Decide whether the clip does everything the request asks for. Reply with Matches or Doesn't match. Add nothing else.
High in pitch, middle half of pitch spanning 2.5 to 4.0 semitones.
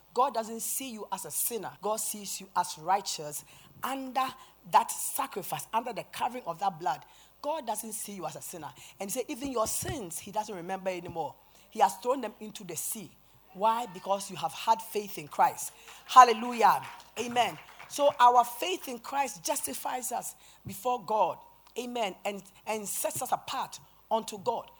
Doesn't match